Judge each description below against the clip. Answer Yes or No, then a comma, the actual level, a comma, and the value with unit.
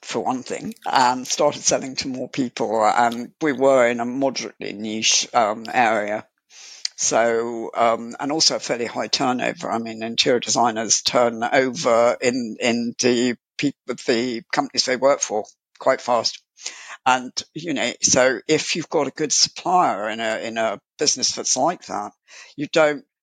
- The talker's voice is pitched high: No, low, 125 Hz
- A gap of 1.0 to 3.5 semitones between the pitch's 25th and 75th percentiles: No, average, 4.0 semitones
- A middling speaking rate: Yes, average, 165 wpm